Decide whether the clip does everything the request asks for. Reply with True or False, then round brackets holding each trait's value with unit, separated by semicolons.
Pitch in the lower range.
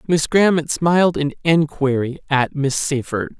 False (150 Hz)